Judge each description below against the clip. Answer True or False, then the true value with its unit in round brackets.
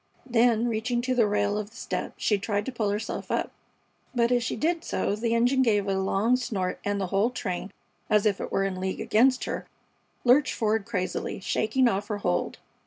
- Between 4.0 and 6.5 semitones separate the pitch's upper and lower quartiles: False (3.2 semitones)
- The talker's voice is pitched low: False (220 Hz)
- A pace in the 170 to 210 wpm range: True (205 wpm)